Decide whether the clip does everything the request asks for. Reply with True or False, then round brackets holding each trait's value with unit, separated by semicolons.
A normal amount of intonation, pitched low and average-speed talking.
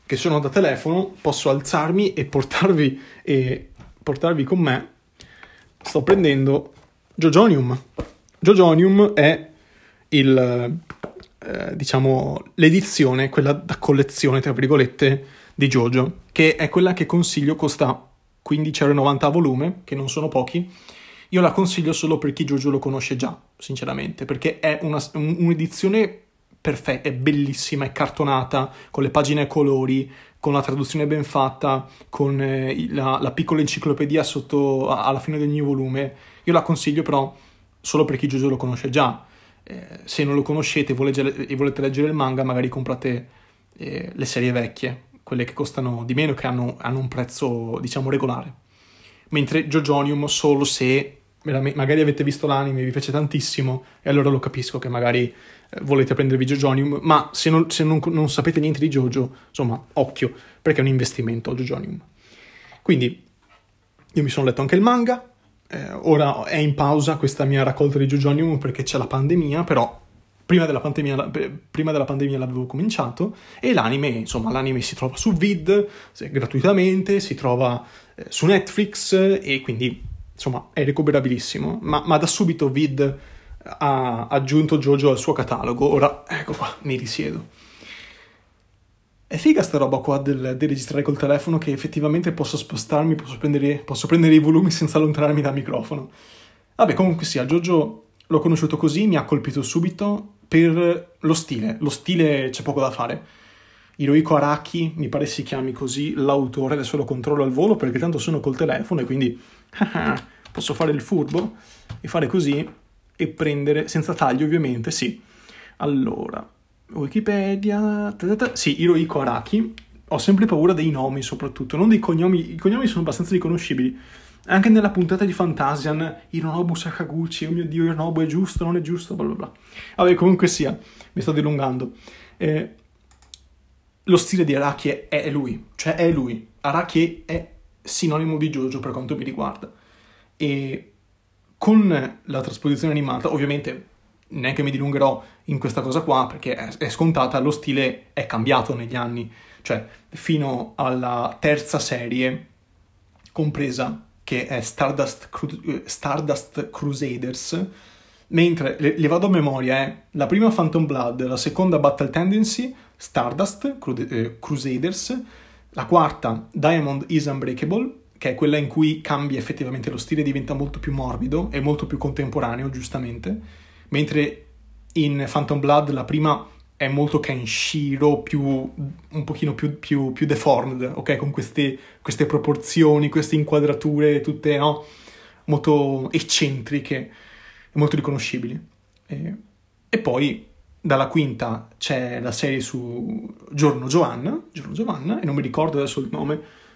False (3.2 semitones; 145 Hz; 150 wpm)